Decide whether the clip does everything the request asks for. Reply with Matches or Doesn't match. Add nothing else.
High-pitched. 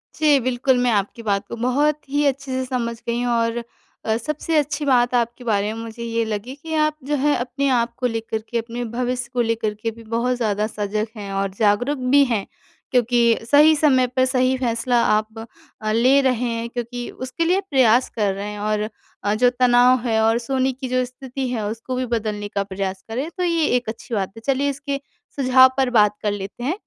Matches